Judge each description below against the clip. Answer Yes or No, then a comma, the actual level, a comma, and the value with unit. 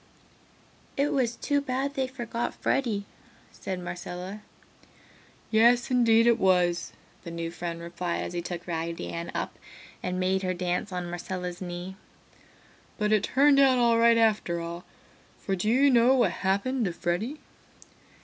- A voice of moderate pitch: No, high, 195 Hz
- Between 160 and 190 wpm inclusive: No, average, 150 wpm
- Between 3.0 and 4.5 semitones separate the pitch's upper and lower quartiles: No, average, 5.3 semitones